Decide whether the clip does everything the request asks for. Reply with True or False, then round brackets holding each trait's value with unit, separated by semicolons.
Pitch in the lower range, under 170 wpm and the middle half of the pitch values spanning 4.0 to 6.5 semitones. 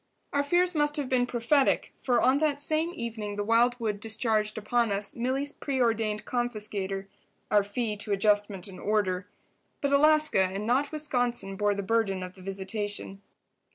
False (225 Hz; 155 wpm; 4.4 semitones)